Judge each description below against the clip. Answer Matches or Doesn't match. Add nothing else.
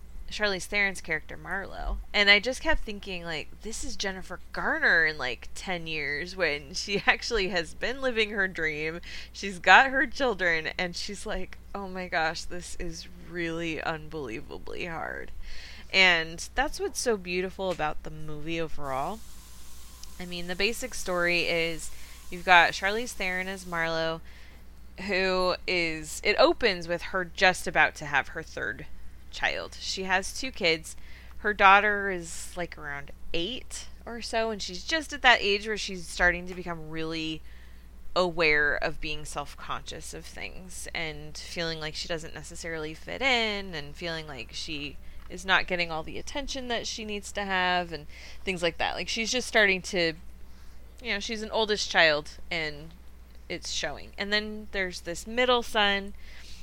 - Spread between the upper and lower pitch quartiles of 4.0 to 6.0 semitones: Matches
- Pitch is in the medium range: Matches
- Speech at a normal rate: Matches